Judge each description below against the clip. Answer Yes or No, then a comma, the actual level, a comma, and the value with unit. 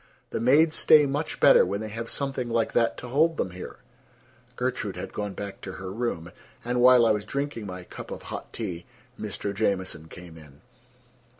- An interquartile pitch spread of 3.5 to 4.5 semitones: No, wide, 5.4 semitones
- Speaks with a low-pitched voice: Yes, low, 110 Hz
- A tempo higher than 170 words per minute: Yes, average, 190 wpm